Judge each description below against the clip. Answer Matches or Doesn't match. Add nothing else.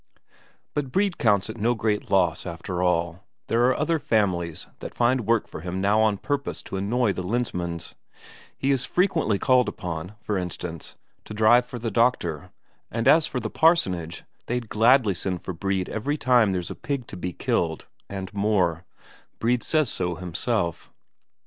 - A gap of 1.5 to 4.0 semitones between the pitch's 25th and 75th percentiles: Doesn't match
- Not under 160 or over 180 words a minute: Matches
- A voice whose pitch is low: Matches